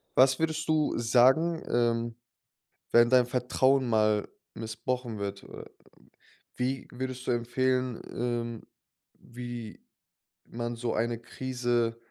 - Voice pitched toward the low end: Yes, low, 120 Hz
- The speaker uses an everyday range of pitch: No, narrow, 1.8 semitones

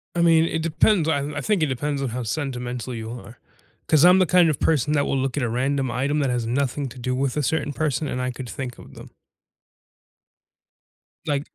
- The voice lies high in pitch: No, medium, 140 Hz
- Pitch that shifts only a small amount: No, average, 3.6 semitones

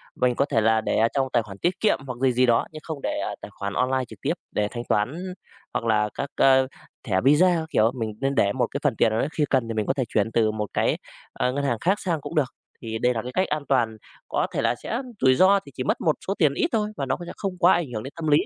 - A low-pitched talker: Yes, low, 130 Hz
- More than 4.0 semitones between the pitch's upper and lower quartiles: Yes, wide, 5.5 semitones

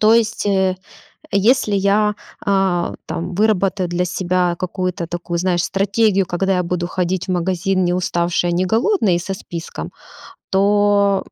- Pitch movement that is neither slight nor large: No, narrow, 2.2 semitones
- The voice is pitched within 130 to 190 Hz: Yes, medium, 185 Hz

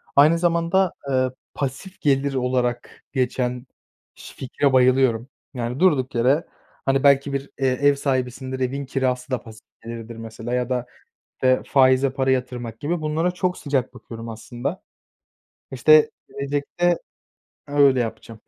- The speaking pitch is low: Yes, low, 130 Hz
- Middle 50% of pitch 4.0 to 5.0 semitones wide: No, narrow, 2.4 semitones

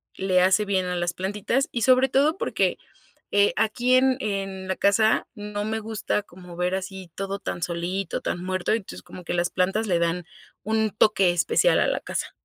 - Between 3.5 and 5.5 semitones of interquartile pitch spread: No, average, 3.1 semitones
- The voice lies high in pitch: Yes, high, 195 Hz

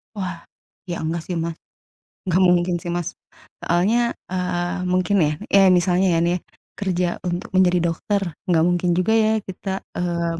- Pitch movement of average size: No, narrow, 1.5 semitones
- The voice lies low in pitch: No, medium, 180 Hz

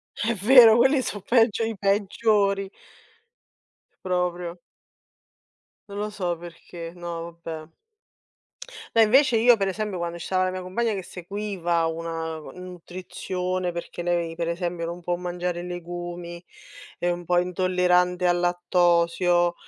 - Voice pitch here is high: No, medium, 180 Hz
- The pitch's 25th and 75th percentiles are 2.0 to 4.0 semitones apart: Yes, narrow, 2.3 semitones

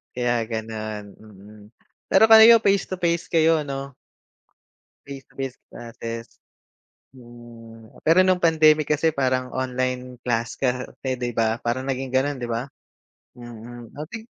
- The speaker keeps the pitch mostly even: No, average, 4.7 semitones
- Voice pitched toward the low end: Yes, low, 125 Hz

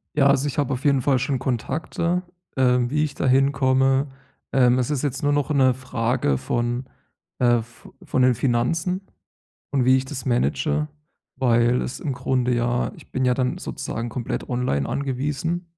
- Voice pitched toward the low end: Yes, low, 130 Hz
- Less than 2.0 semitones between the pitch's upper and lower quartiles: No, narrow, 2.5 semitones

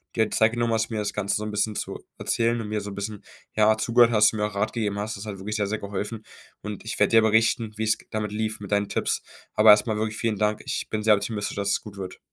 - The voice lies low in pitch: Yes, low, 105 Hz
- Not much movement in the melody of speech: Yes, narrow, 1.2 semitones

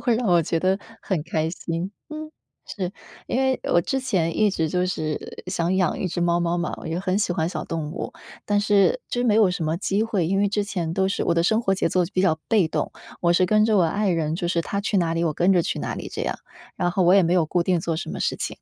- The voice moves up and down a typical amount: Yes, average, 3.2 semitones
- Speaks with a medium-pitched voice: Yes, medium, 180 Hz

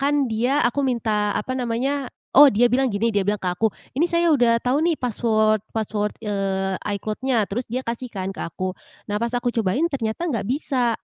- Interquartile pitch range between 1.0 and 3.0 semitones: No, average, 3.7 semitones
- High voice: Yes, high, 230 Hz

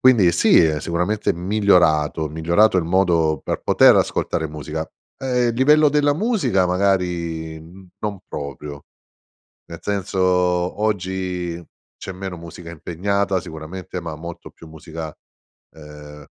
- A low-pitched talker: Yes, very low, 90 Hz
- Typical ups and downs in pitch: Yes, average, 3.6 semitones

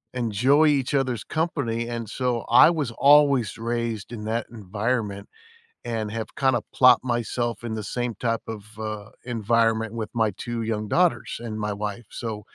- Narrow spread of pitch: Yes, narrow, 2.3 semitones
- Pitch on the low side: Yes, low, 115 Hz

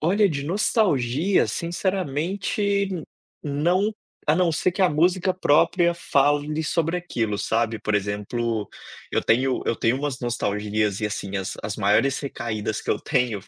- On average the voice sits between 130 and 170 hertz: Yes, medium, 140 Hz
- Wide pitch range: Yes, wide, 8.0 semitones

